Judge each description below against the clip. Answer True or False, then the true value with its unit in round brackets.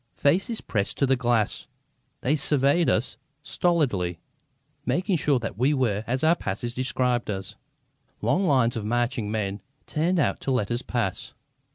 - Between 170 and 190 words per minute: False (155 wpm)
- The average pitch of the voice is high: False (125 Hz)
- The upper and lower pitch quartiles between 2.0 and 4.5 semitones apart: False (5.1 semitones)